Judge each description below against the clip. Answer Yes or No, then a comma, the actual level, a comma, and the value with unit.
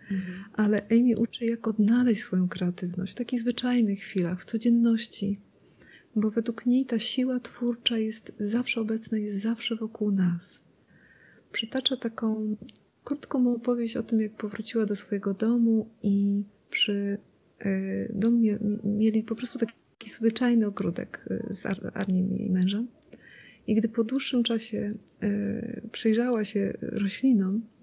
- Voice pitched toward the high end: Yes, high, 220 Hz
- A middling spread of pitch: No, narrow, 2.3 semitones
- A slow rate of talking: No, average, 135 wpm